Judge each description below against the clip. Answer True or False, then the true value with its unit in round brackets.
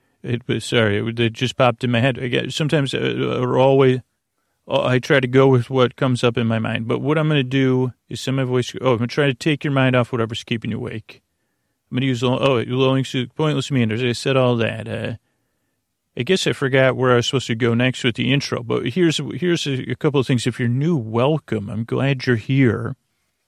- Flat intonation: True (2.3 semitones)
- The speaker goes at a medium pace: False (240 wpm)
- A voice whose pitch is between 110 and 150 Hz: True (130 Hz)